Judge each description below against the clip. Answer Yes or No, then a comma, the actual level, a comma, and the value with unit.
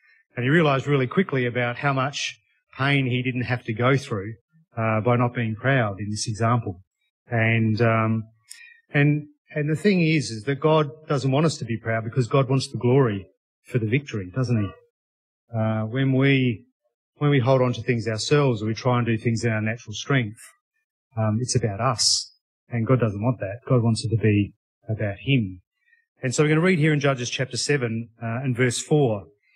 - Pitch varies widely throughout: No, average, 3.8 semitones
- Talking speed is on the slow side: No, fast, 205 wpm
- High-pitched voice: No, low, 125 Hz